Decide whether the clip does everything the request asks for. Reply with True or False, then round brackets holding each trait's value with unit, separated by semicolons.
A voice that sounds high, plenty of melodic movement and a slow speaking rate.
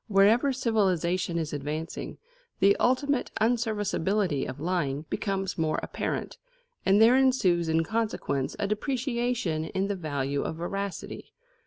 True (195 Hz; 5.8 semitones; 130 wpm)